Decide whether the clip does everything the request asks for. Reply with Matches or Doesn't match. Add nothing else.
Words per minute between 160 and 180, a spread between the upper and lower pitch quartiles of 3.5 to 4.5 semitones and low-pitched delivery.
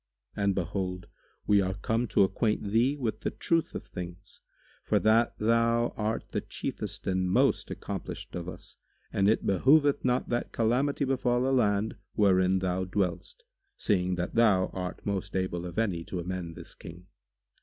Matches